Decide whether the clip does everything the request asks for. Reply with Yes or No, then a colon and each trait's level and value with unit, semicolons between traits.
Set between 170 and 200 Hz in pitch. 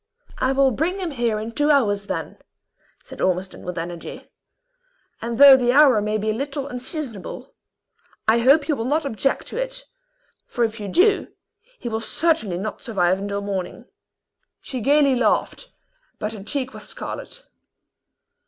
No: high, 240 Hz